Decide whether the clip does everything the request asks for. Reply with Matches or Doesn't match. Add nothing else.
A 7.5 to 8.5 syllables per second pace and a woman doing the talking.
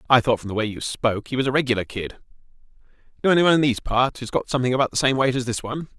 Doesn't match